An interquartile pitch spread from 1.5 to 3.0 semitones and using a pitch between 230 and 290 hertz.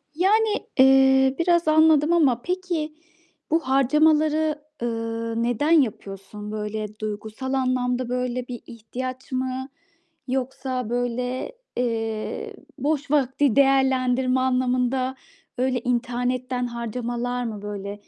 Yes: narrow, 2.4 semitones; very high, 255 Hz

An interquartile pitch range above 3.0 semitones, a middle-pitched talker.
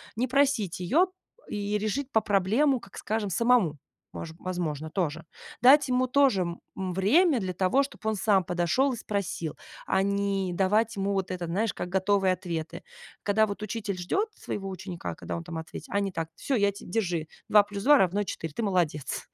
No: average, 3.9 semitones; high, 200 Hz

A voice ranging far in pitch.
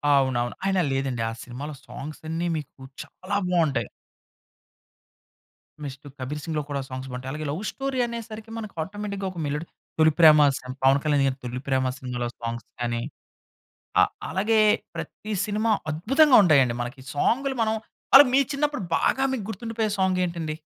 Yes: wide, 8.2 semitones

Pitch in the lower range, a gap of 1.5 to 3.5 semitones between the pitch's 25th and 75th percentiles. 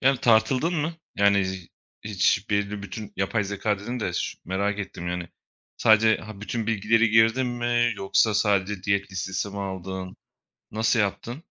Yes: low, 105 Hz; average, 2.7 semitones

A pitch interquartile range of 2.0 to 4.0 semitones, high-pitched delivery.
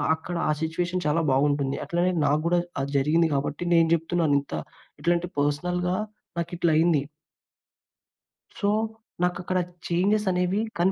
No: average, 3.1 semitones; medium, 170 Hz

